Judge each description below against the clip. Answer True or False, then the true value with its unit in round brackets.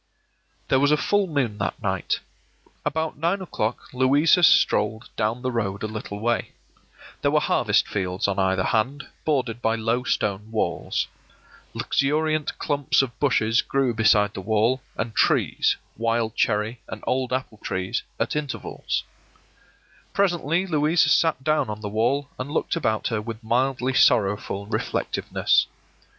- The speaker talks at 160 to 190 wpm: False (150 wpm)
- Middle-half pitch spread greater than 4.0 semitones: True (4.9 semitones)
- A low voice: True (120 Hz)